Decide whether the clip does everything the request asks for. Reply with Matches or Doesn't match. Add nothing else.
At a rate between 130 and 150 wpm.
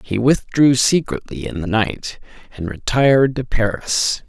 Matches